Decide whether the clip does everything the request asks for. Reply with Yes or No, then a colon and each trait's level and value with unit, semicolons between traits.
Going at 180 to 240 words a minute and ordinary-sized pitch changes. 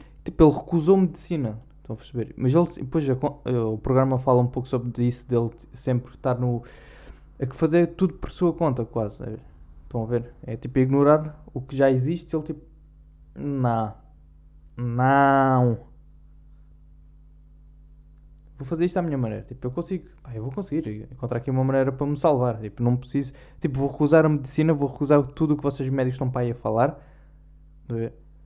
Yes: fast, 185 wpm; average, 4.7 semitones